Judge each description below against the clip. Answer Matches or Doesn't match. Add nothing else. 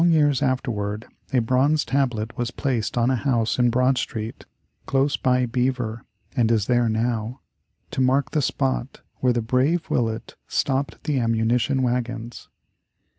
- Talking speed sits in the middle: Matches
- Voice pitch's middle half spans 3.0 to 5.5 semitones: Doesn't match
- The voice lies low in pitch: Matches